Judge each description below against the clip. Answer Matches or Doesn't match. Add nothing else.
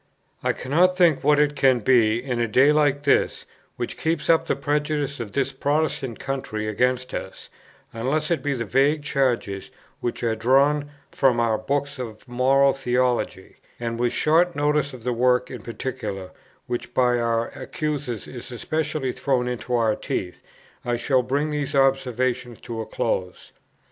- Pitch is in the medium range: Doesn't match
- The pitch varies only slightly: Doesn't match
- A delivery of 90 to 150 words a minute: Doesn't match